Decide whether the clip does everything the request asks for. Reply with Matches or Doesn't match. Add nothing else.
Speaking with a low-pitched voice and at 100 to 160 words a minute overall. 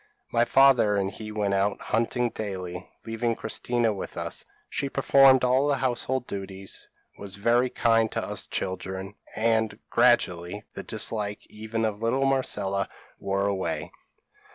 Matches